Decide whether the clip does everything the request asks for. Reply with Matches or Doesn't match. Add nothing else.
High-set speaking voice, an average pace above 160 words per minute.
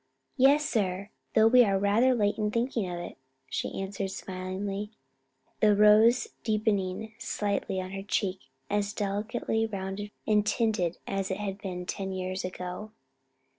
Doesn't match